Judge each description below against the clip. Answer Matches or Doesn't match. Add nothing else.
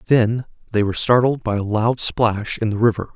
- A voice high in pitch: Doesn't match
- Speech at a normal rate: Doesn't match